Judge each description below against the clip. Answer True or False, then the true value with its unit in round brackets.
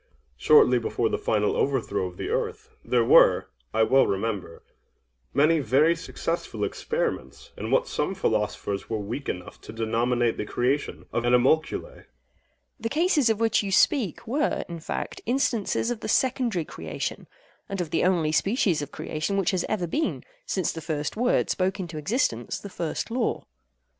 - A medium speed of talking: True (165 wpm)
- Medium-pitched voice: True (165 Hz)